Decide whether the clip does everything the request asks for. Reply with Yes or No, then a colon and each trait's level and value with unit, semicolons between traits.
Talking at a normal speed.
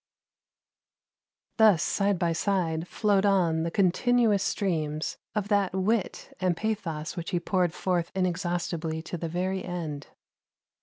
No: slow, 130 wpm